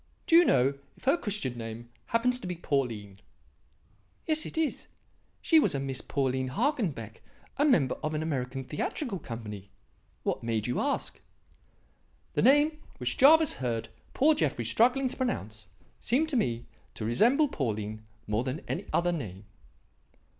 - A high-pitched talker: No, medium, 140 Hz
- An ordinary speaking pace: Yes, average, 155 wpm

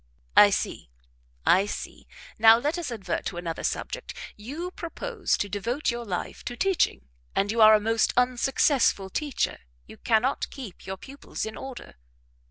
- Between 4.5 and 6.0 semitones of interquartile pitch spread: Yes, average, 5.3 semitones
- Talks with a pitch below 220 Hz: No, high, 235 Hz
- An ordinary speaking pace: Yes, average, 160 wpm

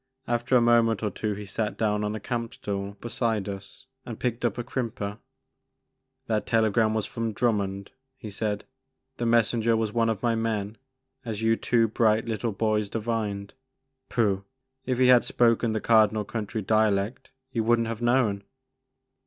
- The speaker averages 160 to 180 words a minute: Yes, average, 170 wpm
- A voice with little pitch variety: Yes, narrow, 2.0 semitones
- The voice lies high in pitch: No, low, 110 Hz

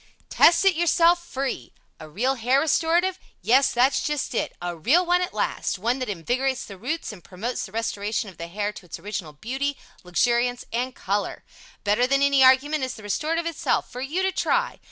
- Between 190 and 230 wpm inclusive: Yes, average, 195 wpm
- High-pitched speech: Yes, very high, 255 Hz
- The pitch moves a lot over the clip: Yes, wide, 6.6 semitones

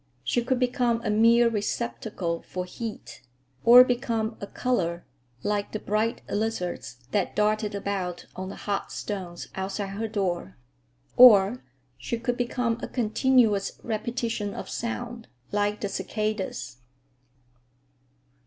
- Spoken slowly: Yes, slow, 125 wpm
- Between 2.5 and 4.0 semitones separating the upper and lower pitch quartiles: Yes, average, 3.1 semitones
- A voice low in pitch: No, high, 215 Hz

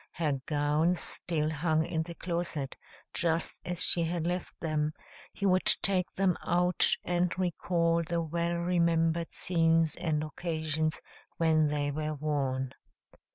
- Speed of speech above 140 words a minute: No, slow, 135 wpm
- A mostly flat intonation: Yes, narrow, 2.1 semitones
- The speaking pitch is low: No, medium, 165 Hz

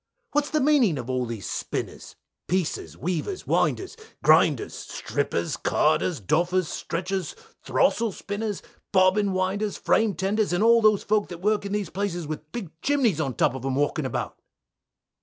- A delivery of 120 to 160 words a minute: Yes, average, 155 wpm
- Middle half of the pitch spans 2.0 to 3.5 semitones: No, average, 4.6 semitones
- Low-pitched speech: No, high, 190 Hz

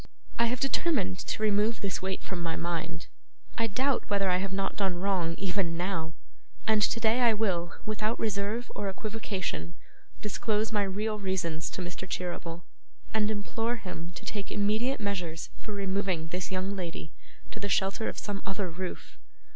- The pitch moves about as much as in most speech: Yes, average, 3.2 semitones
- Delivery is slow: No, average, 165 wpm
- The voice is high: Yes, high, 195 Hz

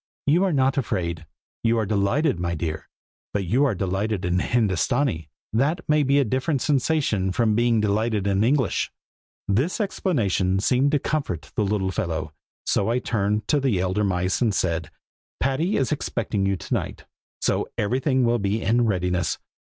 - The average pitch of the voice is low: Yes, low, 110 Hz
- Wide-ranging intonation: Yes, wide, 5.7 semitones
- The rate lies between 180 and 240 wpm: No, average, 170 wpm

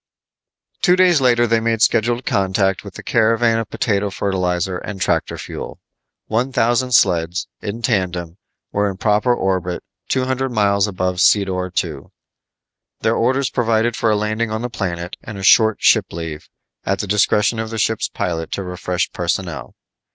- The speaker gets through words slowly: No, average, 165 wpm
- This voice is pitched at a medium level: No, low, 105 Hz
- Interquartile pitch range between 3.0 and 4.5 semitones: Yes, average, 3.9 semitones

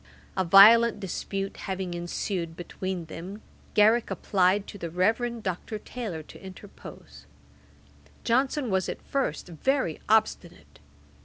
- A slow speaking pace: Yes, slow, 115 wpm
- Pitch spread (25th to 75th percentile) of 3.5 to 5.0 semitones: Yes, average, 4.0 semitones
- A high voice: Yes, high, 195 Hz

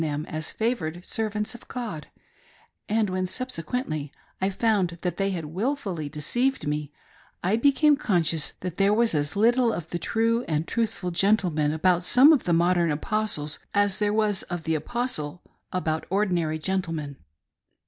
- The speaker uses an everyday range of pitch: No, wide, 5.8 semitones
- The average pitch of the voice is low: No, medium, 185 Hz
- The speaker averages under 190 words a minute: Yes, average, 160 wpm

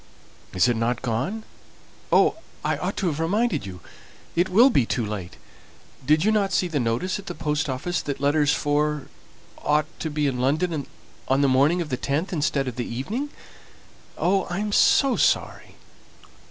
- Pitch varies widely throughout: Yes, wide, 5.7 semitones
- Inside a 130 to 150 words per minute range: No, average, 170 wpm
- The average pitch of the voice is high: No, medium, 150 Hz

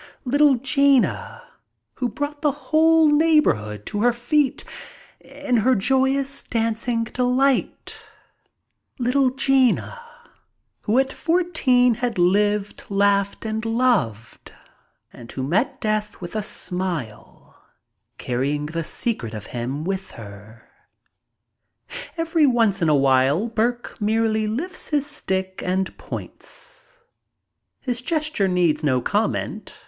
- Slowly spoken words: Yes, slow, 110 wpm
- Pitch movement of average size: No, wide, 6.8 semitones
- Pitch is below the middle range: No, high, 225 Hz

